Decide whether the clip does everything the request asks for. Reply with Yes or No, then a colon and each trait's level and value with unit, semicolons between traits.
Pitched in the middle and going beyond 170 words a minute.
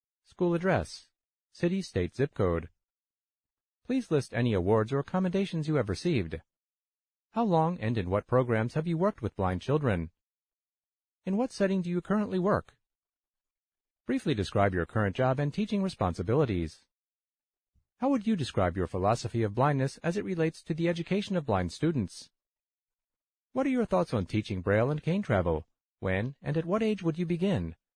No: medium, 145 Hz; average, 165 wpm